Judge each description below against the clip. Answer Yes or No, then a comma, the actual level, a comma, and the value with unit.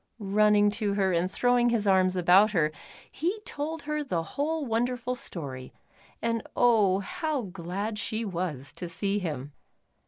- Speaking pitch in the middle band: No, high, 205 Hz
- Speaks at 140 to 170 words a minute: Yes, average, 150 wpm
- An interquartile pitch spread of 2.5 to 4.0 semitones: No, average, 5.1 semitones